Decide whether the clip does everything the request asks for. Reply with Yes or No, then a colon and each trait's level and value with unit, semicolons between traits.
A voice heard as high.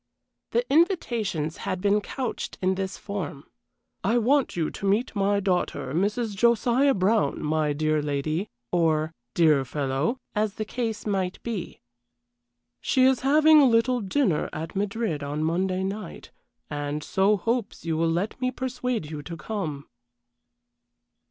Yes: high, 195 Hz